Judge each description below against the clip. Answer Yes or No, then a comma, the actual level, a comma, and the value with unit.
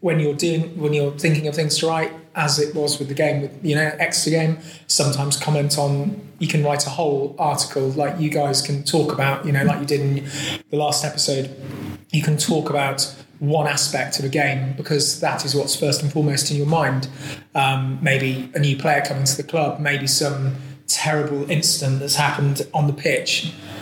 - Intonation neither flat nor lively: No, narrow, 1.7 semitones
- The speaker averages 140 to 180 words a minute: No, fast, 205 wpm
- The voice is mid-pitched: Yes, medium, 145 Hz